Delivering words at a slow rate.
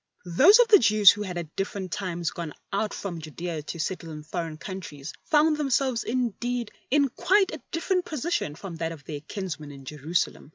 No: average, 190 wpm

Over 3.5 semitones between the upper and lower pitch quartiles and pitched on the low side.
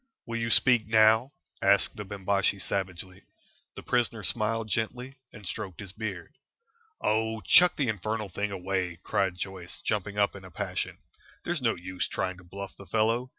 No: average, 3.1 semitones; low, 105 Hz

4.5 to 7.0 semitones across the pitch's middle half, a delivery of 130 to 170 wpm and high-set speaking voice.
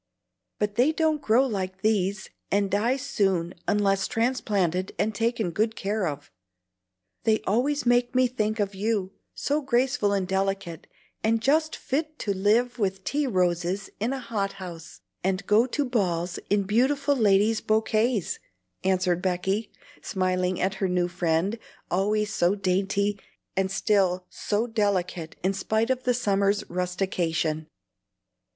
No: average, 3.6 semitones; average, 140 wpm; high, 200 Hz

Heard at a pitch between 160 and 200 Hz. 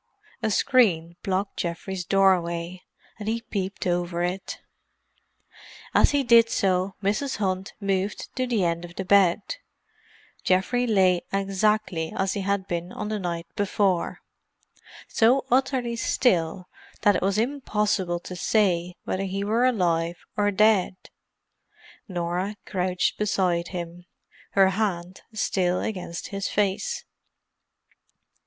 Yes: high, 190 Hz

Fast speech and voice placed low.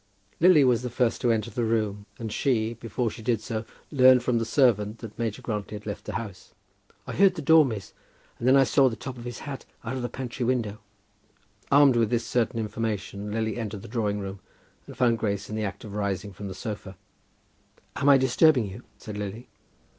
Yes: fast, 215 wpm; low, 115 Hz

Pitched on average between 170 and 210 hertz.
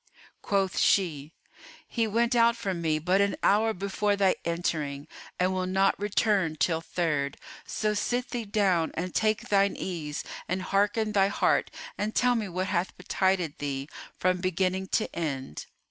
Yes: high, 190 Hz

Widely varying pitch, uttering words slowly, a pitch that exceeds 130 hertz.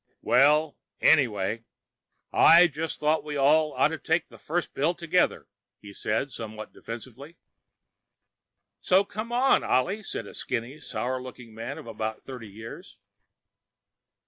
Yes: wide, 6.0 semitones; slow, 130 wpm; medium, 140 Hz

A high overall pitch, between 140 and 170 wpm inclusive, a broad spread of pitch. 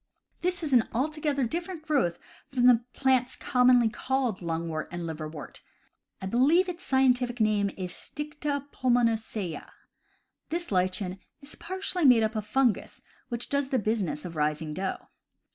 Yes: high, 245 Hz; average, 150 wpm; wide, 6.8 semitones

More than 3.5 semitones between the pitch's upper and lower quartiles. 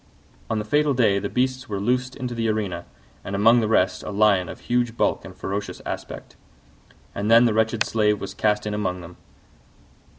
No: average, 3.0 semitones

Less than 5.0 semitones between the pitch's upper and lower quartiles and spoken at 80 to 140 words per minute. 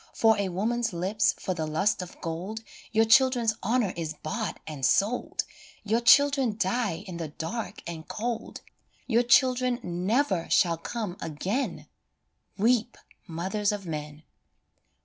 No: wide, 5.6 semitones; slow, 135 wpm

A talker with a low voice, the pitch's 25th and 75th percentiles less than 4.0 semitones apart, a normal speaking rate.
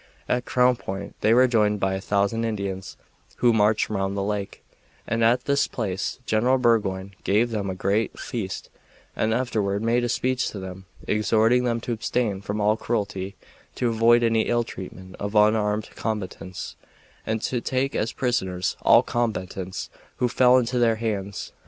Yes: low, 110 Hz; average, 3.1 semitones; average, 165 wpm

